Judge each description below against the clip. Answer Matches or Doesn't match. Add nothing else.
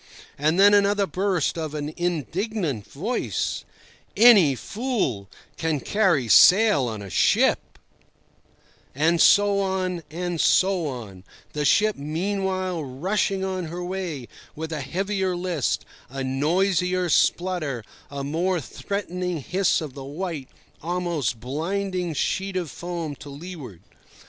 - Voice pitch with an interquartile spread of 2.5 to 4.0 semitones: Doesn't match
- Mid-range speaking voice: Matches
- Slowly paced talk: Matches